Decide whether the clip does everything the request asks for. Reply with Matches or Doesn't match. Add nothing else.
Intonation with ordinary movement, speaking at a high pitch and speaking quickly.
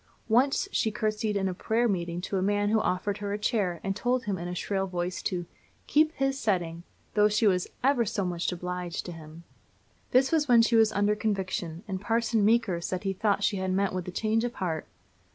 Matches